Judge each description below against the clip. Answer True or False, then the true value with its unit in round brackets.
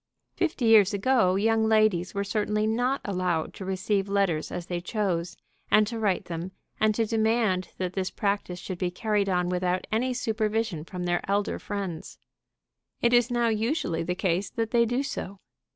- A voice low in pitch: False (200 Hz)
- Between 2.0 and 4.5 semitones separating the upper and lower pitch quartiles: True (3.5 semitones)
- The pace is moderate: True (175 wpm)